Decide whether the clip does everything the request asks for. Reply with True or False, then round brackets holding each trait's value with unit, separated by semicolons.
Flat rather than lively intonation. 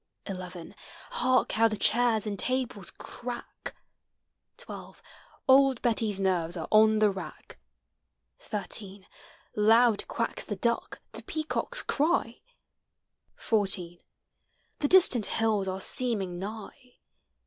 False (4.1 semitones)